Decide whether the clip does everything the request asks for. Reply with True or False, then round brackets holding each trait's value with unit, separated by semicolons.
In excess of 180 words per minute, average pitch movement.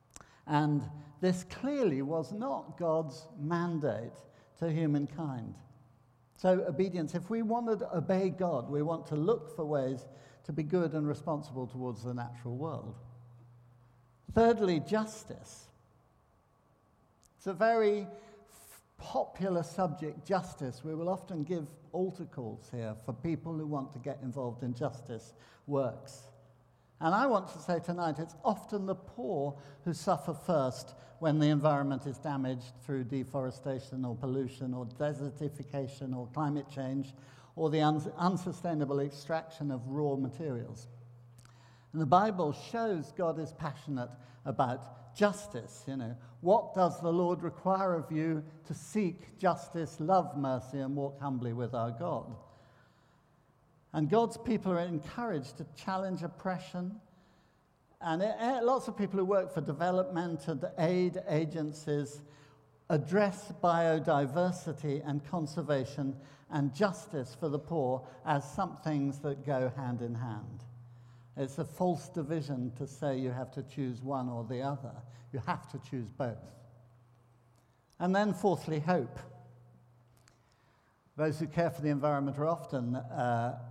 False (135 wpm; 4.8 semitones)